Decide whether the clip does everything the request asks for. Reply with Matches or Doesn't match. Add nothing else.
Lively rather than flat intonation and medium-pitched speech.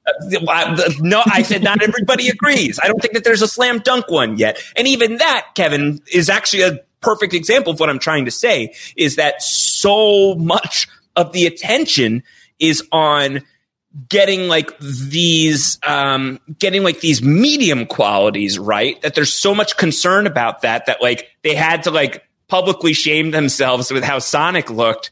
Matches